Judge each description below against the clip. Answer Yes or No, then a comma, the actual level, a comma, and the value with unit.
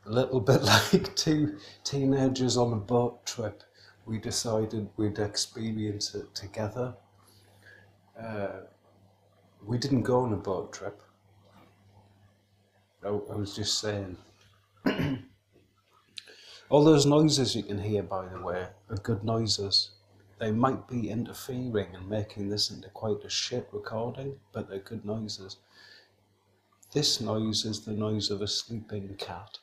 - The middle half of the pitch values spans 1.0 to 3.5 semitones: Yes, narrow, 2.6 semitones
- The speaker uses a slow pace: Yes, slow, 130 wpm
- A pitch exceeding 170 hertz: No, low, 105 Hz